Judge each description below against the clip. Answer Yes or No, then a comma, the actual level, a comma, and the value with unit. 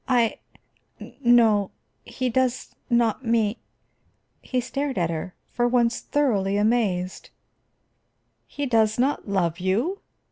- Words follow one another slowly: Yes, slow, 115 wpm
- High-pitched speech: Yes, high, 230 Hz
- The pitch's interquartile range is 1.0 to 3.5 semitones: No, average, 4.0 semitones